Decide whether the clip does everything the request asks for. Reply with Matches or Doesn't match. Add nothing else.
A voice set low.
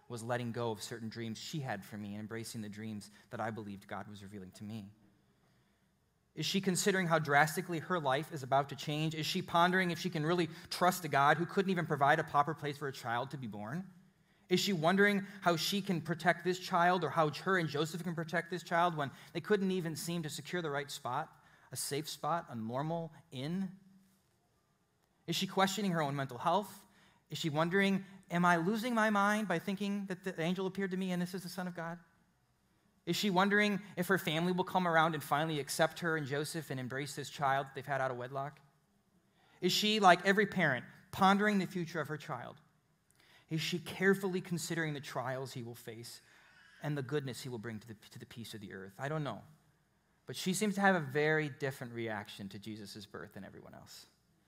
Doesn't match